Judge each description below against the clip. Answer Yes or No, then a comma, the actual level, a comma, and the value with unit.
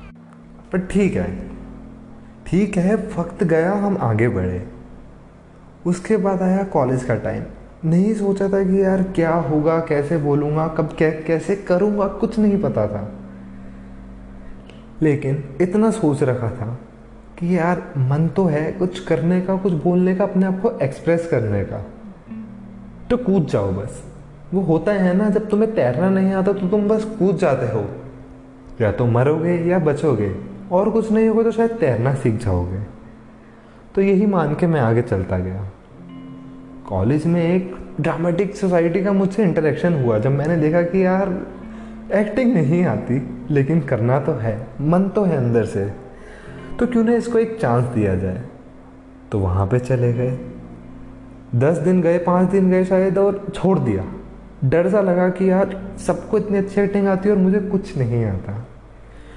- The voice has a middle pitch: Yes, medium, 165 Hz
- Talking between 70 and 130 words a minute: No, average, 160 wpm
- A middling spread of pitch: No, wide, 8.8 semitones